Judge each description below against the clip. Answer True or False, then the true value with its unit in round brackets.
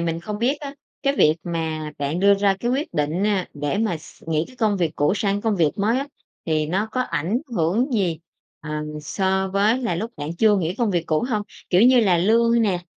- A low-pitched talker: False (195 Hz)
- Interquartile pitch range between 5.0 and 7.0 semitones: True (5.4 semitones)